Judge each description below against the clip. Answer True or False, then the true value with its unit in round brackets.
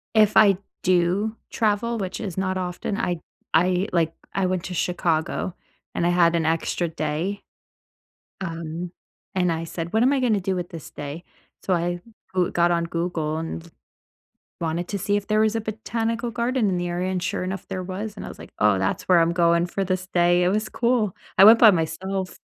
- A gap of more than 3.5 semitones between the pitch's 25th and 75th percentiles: False (3.1 semitones)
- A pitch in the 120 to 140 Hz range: False (180 Hz)